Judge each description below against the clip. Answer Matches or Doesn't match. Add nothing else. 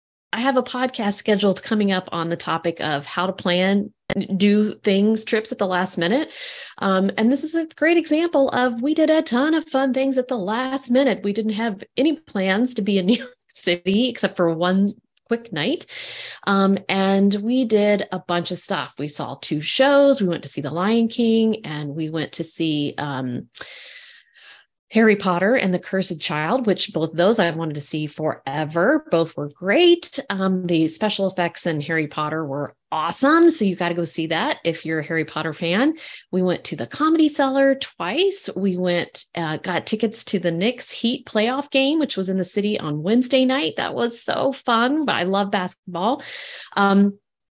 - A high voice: Matches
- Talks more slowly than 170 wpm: Doesn't match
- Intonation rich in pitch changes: Matches